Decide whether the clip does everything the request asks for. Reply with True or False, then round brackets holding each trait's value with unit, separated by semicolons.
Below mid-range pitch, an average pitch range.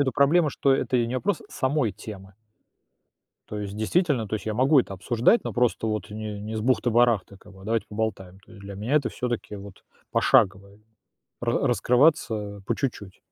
True (110 Hz; 4.1 semitones)